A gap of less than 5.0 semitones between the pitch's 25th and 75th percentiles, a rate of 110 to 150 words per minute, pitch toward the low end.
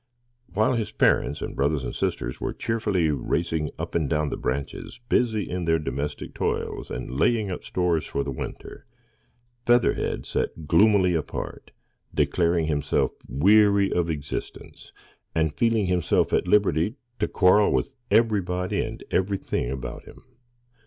No: average, 5.3 semitones; average, 140 wpm; very low, 90 Hz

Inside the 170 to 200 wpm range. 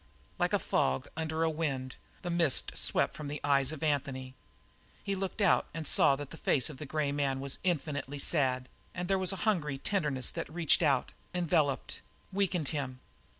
Yes: average, 185 wpm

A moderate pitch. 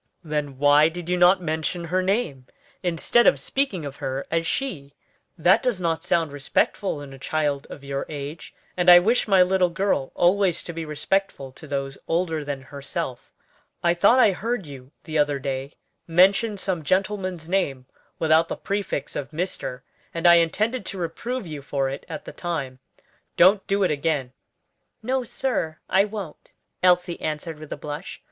Yes: medium, 165 Hz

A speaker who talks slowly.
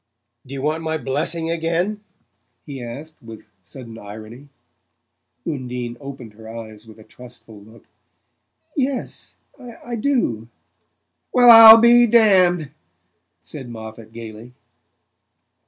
Yes: slow, 110 wpm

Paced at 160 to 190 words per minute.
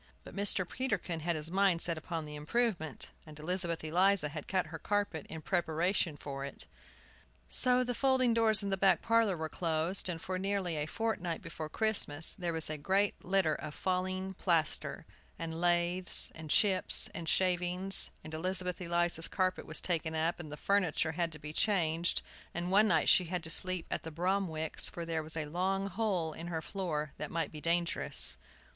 Yes: average, 185 wpm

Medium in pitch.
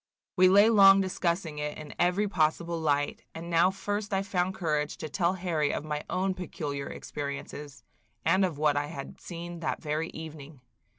Yes: medium, 165 Hz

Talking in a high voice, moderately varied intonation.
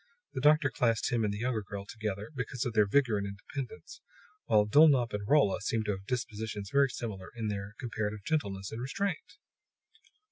No: low, 110 Hz; average, 3.9 semitones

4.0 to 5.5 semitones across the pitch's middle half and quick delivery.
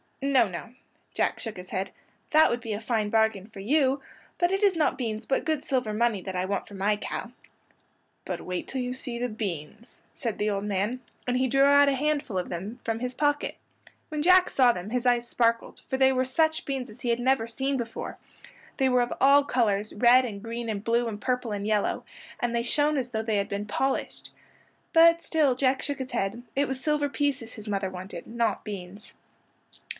Yes: average, 4.3 semitones; fast, 215 wpm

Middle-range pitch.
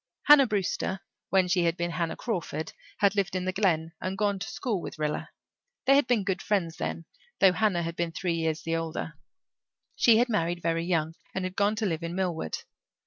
Yes: medium, 180 Hz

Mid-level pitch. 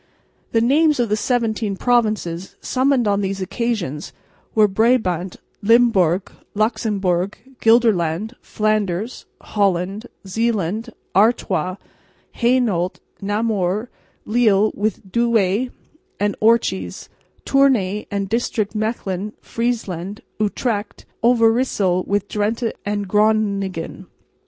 No: high, 210 Hz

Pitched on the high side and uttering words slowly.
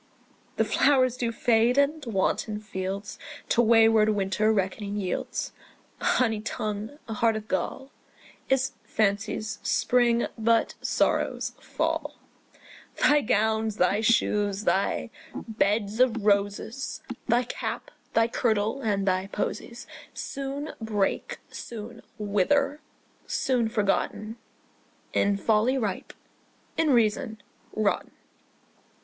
Yes: high, 220 Hz; slow, 105 wpm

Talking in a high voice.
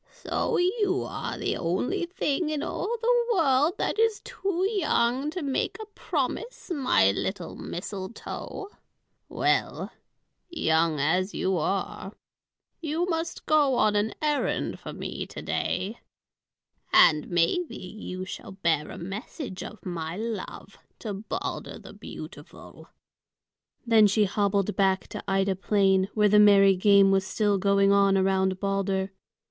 Yes: high, 205 Hz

